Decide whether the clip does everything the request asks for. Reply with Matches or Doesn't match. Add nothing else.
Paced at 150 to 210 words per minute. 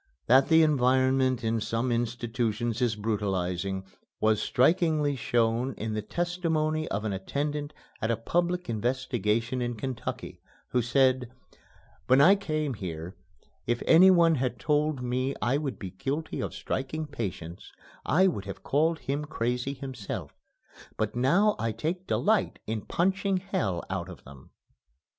Doesn't match